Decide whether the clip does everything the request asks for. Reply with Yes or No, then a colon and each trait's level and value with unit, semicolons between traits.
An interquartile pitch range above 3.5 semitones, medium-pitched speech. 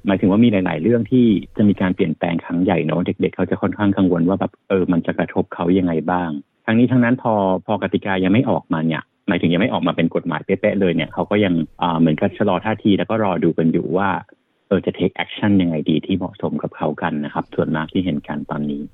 No: average, 3.9 semitones; very low, 95 Hz